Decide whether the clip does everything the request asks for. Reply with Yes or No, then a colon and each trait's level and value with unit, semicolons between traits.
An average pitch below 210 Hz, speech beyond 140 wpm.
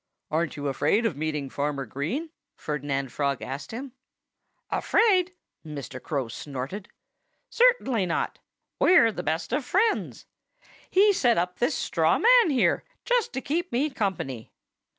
No: medium, 185 Hz; slow, 135 wpm